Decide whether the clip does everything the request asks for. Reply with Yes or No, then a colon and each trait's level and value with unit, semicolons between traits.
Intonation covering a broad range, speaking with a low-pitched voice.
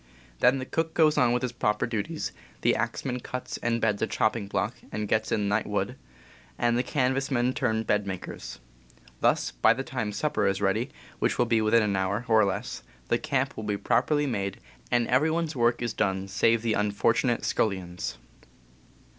No: average, 3.5 semitones; low, 115 Hz